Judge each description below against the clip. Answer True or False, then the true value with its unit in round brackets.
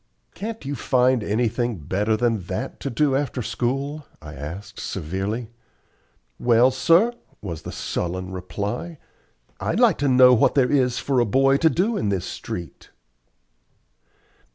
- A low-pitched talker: True (120 Hz)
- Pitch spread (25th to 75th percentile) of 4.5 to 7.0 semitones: True (5.2 semitones)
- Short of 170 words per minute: True (145 wpm)